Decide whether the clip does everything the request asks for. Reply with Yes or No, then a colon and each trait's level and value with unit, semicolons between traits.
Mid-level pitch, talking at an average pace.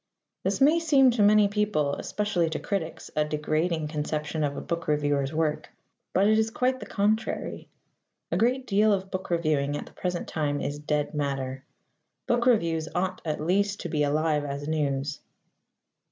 Yes: medium, 160 Hz; average, 170 wpm